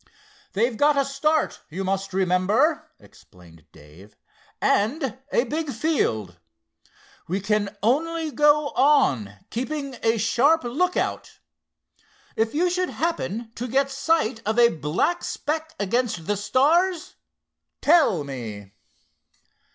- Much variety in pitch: Yes, wide, 7.8 semitones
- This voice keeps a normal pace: No, slow, 115 wpm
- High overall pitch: Yes, high, 240 Hz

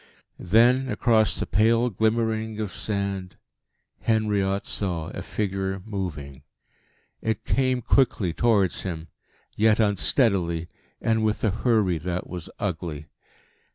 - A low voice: Yes, low, 100 Hz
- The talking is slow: Yes, slow, 115 wpm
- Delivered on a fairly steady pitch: No, average, 3.5 semitones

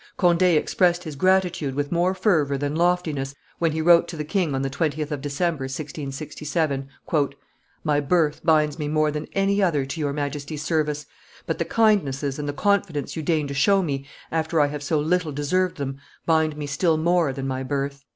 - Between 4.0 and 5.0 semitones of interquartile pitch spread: No, average, 3.2 semitones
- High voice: No, medium, 150 Hz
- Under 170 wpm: No, average, 190 wpm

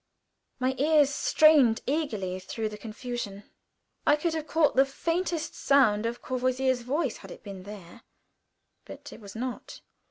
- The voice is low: No, very high, 255 Hz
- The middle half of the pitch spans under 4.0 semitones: No, wide, 5.5 semitones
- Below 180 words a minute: Yes, average, 150 wpm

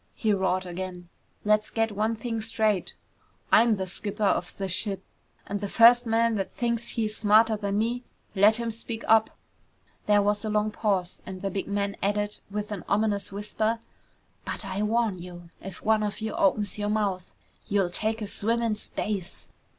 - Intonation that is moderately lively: No, narrow, 2.0 semitones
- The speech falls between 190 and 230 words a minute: No, average, 180 wpm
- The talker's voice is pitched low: No, high, 210 Hz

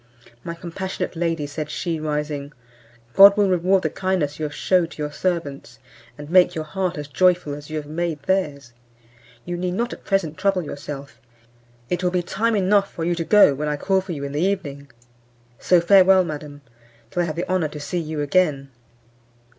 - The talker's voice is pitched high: No, medium, 170 Hz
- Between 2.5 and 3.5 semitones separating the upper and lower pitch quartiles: No, average, 3.9 semitones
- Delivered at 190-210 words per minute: Yes, average, 195 wpm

